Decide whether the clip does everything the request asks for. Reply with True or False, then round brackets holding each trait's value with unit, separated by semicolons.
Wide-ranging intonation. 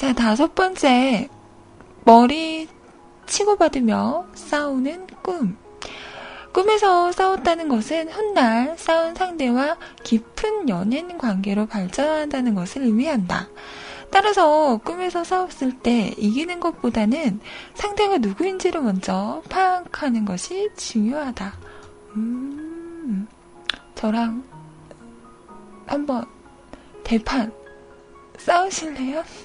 True (7.3 semitones)